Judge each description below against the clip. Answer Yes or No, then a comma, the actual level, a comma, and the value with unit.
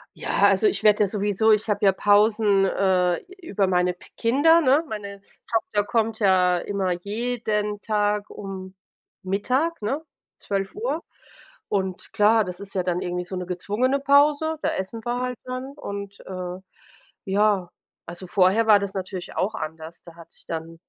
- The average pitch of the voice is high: Yes, high, 205 Hz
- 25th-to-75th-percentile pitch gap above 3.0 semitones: Yes, average, 3.4 semitones